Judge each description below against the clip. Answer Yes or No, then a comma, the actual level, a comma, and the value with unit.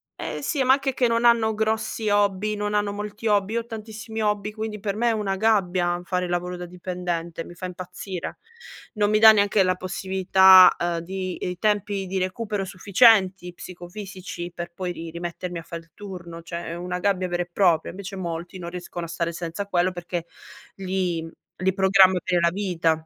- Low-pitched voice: No, medium, 185 Hz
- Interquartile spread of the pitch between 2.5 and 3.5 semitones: Yes, average, 2.9 semitones